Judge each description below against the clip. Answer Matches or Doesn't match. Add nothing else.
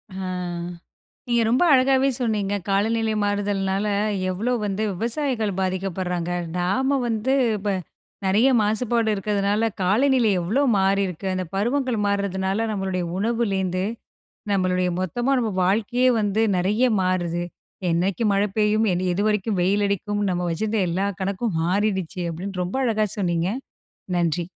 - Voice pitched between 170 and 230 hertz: Matches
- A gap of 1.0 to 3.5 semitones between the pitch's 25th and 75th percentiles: Matches